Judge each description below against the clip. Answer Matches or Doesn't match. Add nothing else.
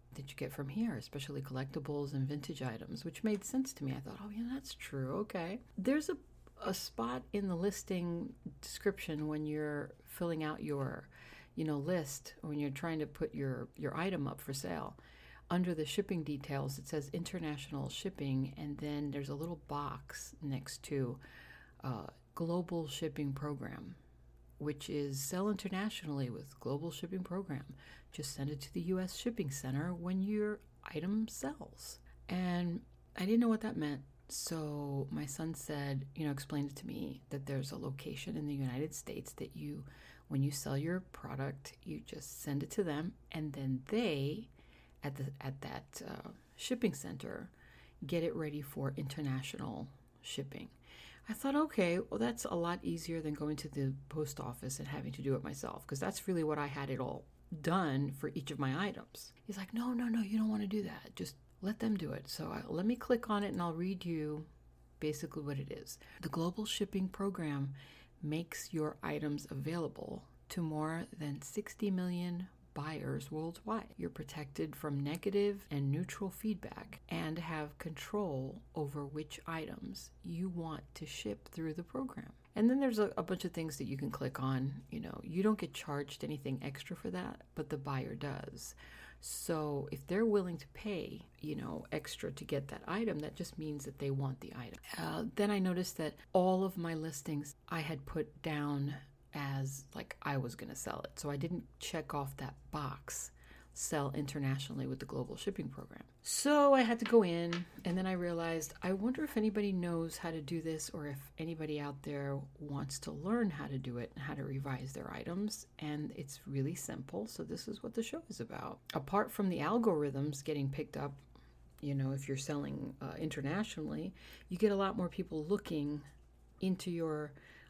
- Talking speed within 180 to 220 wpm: Matches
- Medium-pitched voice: Matches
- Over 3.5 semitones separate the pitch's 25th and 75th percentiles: Matches